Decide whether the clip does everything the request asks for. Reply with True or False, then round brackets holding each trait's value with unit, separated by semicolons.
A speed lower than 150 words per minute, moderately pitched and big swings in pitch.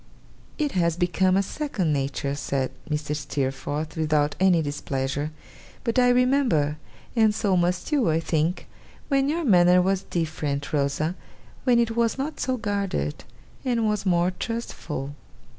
True (140 wpm; 175 Hz; 7.3 semitones)